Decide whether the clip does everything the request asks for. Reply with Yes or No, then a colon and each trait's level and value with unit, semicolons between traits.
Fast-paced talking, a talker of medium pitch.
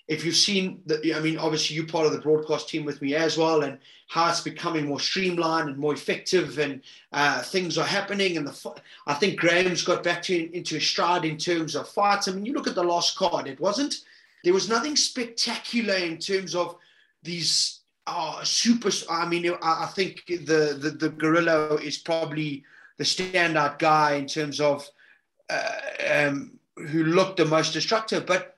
No: average, 190 wpm; medium, 165 Hz